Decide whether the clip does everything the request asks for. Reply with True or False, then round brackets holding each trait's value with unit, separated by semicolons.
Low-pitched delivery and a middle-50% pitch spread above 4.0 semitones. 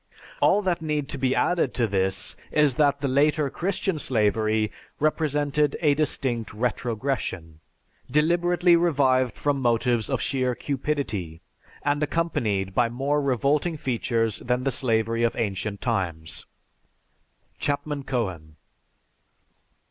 True (130 Hz; 4.8 semitones)